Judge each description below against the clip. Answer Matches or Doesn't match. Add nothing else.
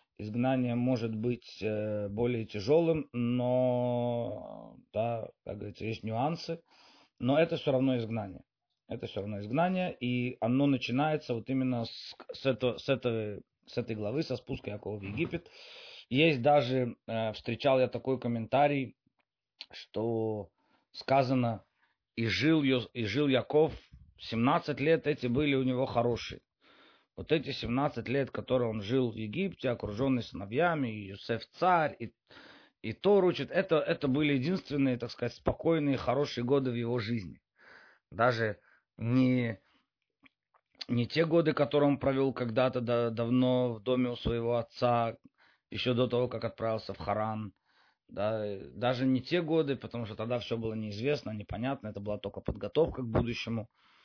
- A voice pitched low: Matches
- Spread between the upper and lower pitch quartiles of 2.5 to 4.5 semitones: Matches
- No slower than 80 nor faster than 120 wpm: Doesn't match